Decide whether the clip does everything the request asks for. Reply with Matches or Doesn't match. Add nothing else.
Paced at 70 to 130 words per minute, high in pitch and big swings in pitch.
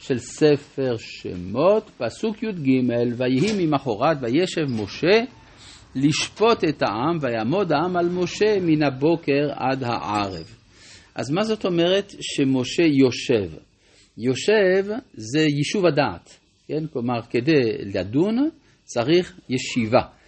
Doesn't match